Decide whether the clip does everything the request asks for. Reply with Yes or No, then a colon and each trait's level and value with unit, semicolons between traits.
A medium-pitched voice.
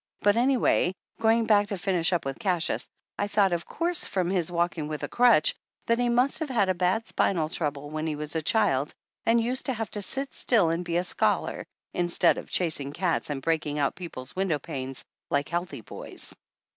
Yes: medium, 180 Hz